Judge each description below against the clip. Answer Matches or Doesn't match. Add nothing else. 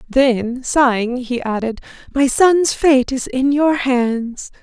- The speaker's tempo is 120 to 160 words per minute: Matches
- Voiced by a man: Doesn't match